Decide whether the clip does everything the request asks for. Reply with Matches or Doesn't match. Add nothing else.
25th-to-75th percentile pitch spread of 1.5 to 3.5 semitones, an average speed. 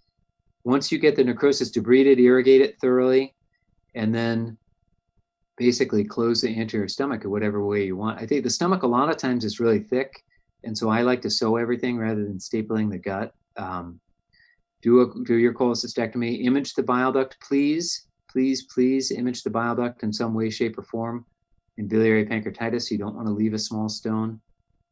Matches